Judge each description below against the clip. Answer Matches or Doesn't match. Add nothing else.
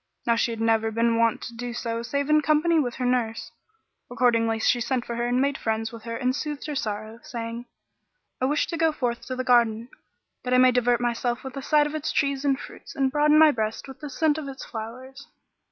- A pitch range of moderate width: Matches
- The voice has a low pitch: Doesn't match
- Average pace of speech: Doesn't match